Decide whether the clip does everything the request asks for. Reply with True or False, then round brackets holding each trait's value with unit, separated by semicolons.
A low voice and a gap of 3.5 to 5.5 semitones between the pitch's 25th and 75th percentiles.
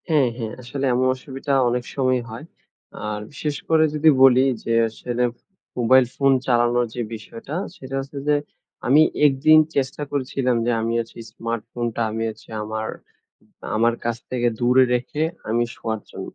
False (125 Hz; 2.6 semitones)